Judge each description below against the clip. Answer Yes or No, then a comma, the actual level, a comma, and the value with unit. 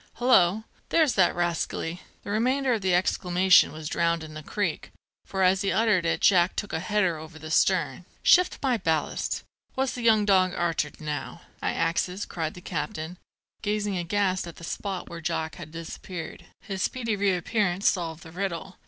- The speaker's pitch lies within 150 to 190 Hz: Yes, medium, 185 Hz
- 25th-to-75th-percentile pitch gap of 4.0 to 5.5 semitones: No, average, 3.6 semitones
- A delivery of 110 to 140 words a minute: No, average, 180 wpm